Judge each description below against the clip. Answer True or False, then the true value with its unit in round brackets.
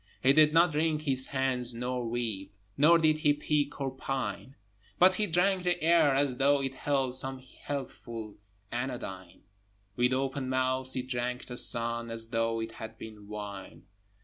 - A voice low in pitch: True (130 Hz)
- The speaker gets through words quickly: False (165 wpm)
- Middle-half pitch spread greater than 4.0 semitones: False (3.7 semitones)